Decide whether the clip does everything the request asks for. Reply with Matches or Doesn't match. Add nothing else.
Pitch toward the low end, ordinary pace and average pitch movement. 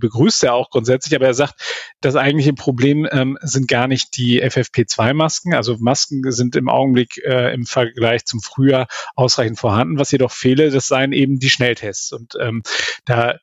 Doesn't match